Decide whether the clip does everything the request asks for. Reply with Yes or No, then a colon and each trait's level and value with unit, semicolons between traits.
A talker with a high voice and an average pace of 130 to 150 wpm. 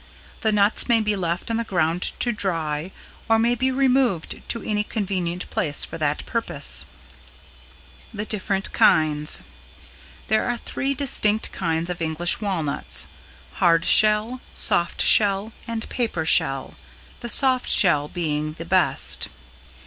Yes: high, 195 Hz; average, 140 wpm